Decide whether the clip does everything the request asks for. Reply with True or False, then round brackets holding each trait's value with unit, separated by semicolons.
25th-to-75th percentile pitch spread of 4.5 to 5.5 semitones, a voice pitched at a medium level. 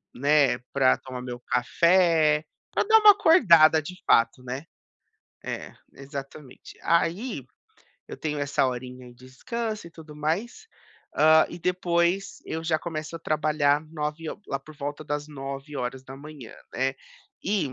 False (3.7 semitones; 150 Hz)